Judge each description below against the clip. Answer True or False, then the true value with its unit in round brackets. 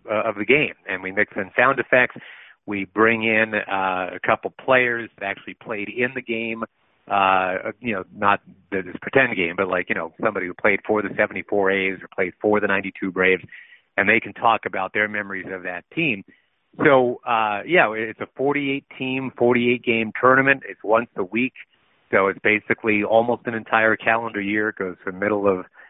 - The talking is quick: False (195 wpm)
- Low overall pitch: True (105 Hz)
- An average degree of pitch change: True (3.4 semitones)